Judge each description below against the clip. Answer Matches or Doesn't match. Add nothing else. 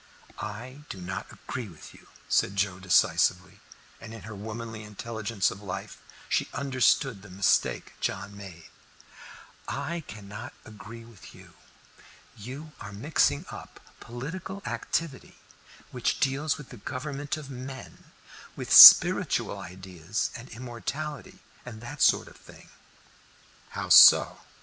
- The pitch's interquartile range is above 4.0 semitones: Matches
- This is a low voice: Matches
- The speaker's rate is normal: Doesn't match